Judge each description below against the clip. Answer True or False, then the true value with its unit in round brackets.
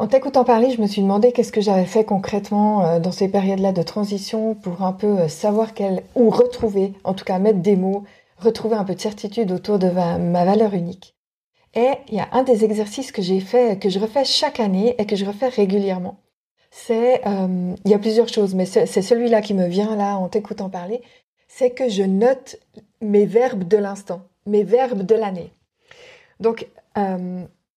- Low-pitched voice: False (210 Hz)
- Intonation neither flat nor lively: True (3.2 semitones)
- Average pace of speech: True (200 wpm)